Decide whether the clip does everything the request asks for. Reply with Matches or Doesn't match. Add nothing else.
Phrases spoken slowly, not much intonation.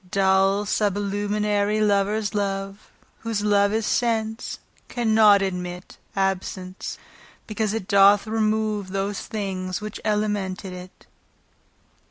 Matches